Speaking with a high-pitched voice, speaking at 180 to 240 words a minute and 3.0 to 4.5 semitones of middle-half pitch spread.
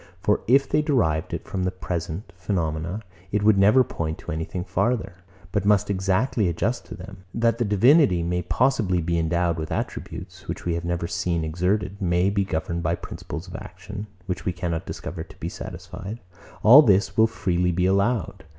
No: very low, 95 Hz; average, 185 wpm; average, 3.3 semitones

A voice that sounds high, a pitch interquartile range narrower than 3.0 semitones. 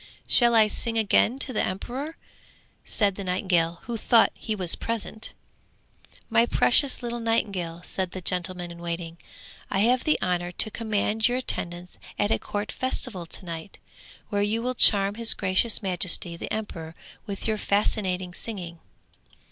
No: high, 200 Hz; average, 4.2 semitones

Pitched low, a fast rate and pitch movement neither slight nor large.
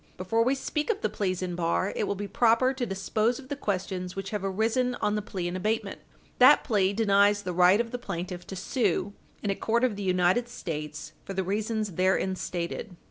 No: high, 200 Hz; fast, 215 wpm; average, 3.6 semitones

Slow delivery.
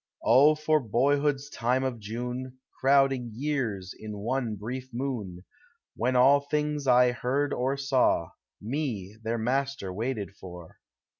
Yes: slow, 130 wpm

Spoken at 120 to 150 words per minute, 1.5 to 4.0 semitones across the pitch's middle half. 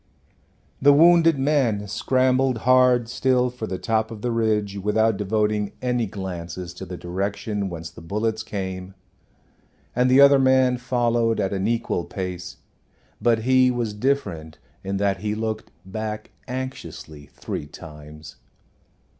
No: average, 140 wpm; average, 4.8 semitones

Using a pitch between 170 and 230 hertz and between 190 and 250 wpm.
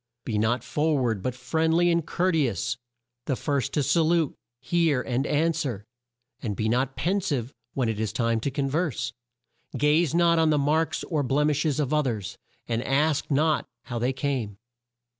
No: medium, 140 Hz; average, 195 wpm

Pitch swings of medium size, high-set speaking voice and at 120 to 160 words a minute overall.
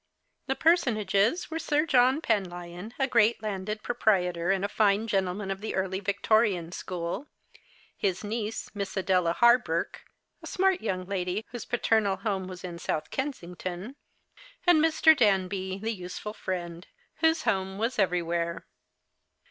Yes: average, 4.3 semitones; high, 200 Hz; average, 140 wpm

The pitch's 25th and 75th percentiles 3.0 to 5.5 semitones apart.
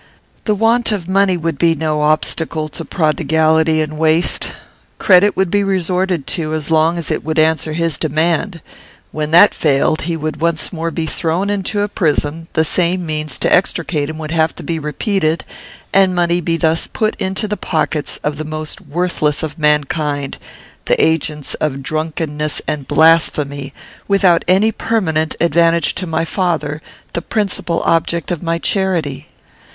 No: narrow, 2.6 semitones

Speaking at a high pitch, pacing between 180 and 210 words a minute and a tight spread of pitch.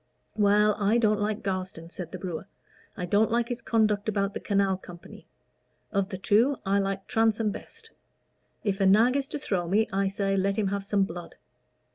Yes: high, 200 Hz; average, 190 wpm; narrow, 2.1 semitones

